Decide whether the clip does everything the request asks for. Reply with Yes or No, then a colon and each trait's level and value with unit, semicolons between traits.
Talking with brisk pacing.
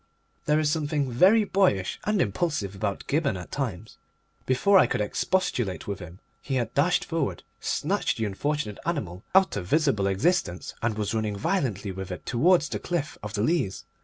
No: average, 175 wpm